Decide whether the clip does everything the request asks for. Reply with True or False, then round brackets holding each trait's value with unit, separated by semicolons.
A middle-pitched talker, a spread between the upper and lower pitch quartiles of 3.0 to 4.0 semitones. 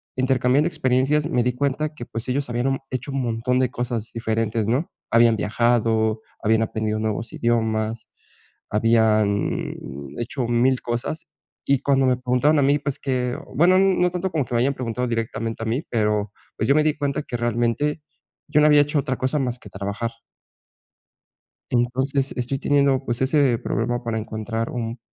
False (125 Hz; 3.3 semitones)